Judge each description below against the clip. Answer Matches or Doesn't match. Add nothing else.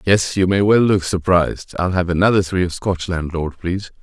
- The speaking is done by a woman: Doesn't match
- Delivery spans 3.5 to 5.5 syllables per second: Matches